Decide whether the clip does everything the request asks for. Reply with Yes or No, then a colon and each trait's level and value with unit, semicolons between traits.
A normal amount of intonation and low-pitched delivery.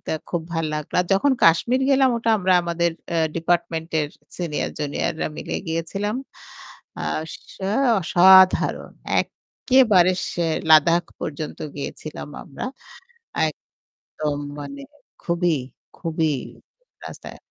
No: average, 3.0 semitones; medium, 170 Hz